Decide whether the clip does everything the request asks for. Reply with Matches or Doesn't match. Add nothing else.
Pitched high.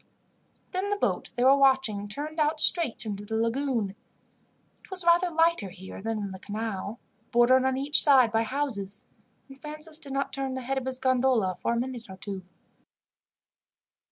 Matches